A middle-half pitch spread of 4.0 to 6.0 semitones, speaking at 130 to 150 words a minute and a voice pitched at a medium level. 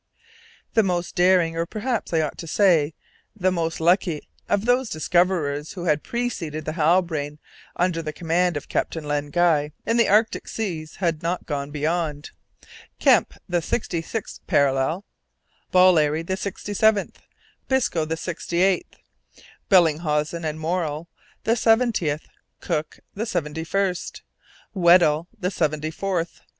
No: average, 3.4 semitones; average, 140 wpm; medium, 170 Hz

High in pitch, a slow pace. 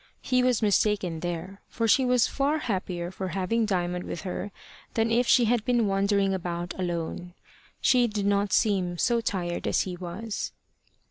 No: high, 200 Hz; average, 170 wpm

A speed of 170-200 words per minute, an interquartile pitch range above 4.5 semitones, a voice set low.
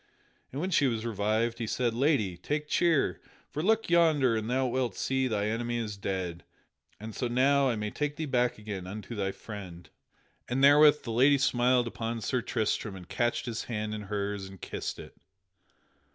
No: average, 185 wpm; average, 4.1 semitones; low, 120 Hz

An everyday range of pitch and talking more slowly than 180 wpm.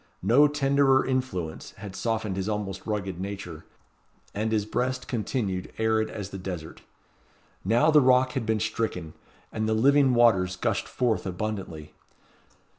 Yes: average, 4.8 semitones; average, 140 wpm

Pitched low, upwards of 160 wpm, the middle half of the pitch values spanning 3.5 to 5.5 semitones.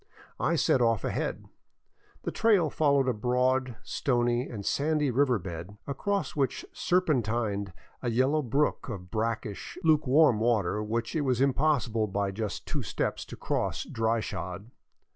No: low, 120 Hz; average, 145 wpm; average, 4.8 semitones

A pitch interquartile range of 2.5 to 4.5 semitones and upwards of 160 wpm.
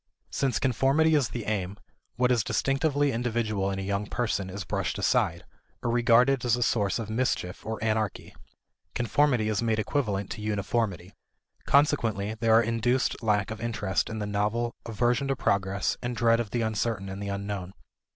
Yes: average, 3.1 semitones; average, 170 wpm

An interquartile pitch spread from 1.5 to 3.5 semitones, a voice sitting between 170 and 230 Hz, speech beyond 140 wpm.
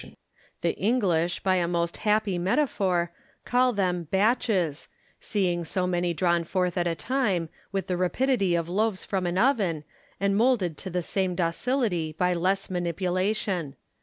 Yes: average, 3.0 semitones; medium, 185 Hz; average, 150 wpm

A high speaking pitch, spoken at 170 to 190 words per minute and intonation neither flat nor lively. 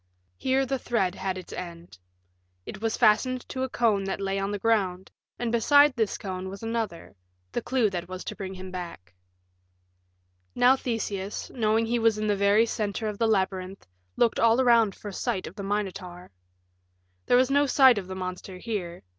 Yes: high, 205 Hz; average, 185 wpm; average, 3.7 semitones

